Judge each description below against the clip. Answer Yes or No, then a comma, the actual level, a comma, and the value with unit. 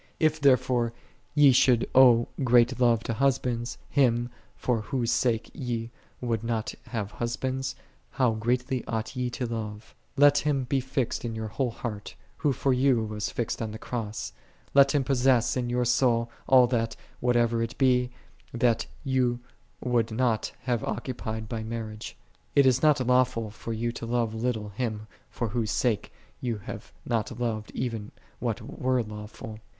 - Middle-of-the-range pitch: No, low, 120 Hz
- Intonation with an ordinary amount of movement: No, narrow, 2.2 semitones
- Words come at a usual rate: Yes, average, 165 wpm